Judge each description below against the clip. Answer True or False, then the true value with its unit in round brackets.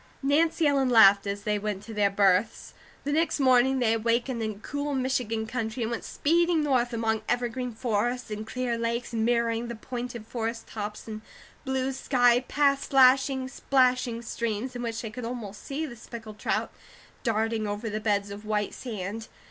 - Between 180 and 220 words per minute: False (170 wpm)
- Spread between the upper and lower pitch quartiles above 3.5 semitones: False (2.9 semitones)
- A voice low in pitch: False (235 Hz)